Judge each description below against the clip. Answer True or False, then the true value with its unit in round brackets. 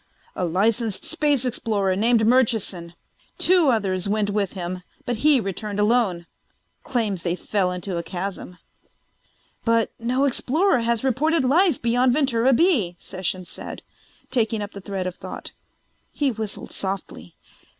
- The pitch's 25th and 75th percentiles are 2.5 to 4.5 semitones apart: False (5.0 semitones)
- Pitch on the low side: False (220 Hz)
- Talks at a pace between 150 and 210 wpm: False (140 wpm)